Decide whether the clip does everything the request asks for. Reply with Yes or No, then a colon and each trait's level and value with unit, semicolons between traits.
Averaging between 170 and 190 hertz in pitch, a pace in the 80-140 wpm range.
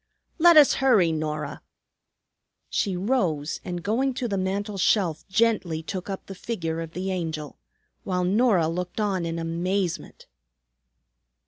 Yes: medium, 185 Hz; slow, 135 wpm